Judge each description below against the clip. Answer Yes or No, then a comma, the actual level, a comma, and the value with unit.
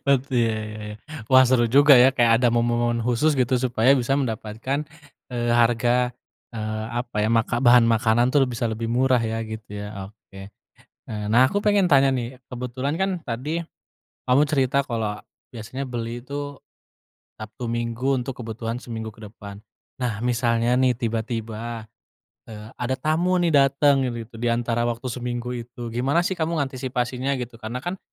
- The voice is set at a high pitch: No, low, 120 Hz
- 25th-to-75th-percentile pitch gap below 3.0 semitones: Yes, narrow, 2.5 semitones